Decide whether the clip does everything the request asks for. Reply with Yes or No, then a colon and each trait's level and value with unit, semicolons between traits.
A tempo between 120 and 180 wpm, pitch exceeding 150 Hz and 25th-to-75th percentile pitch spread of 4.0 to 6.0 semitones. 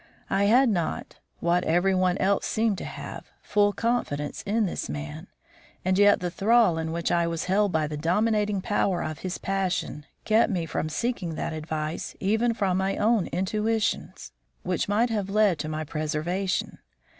Yes: average, 170 wpm; high, 190 Hz; average, 4.4 semitones